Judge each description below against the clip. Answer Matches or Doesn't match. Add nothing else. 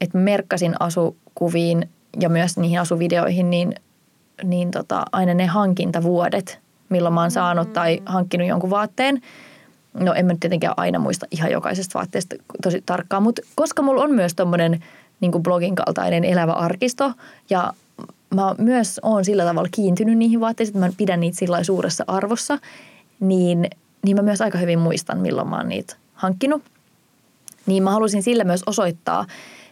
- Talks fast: Matches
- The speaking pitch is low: Doesn't match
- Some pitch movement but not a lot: Matches